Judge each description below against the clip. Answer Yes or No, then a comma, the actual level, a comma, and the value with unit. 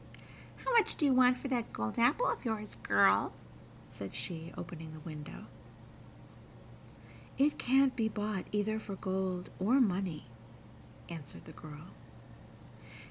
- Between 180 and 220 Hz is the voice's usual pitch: Yes, high, 190 Hz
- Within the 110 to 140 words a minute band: Yes, slow, 135 wpm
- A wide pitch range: Yes, wide, 7.7 semitones